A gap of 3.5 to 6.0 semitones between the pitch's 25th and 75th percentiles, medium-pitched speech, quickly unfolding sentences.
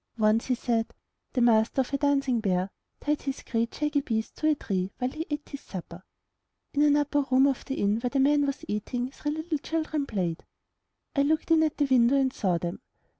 No: average, 4.7 semitones; very high, 265 Hz; fast, 215 wpm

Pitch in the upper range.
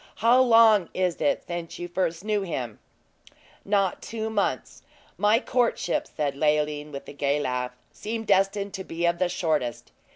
No: medium, 180 Hz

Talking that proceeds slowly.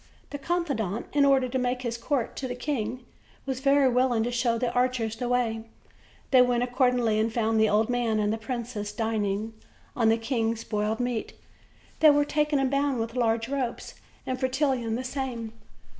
No: average, 185 wpm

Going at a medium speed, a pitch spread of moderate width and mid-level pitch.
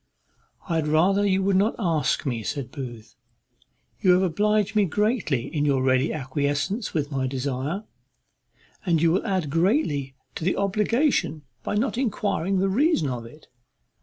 No: average, 160 wpm; wide, 6.0 semitones; medium, 165 Hz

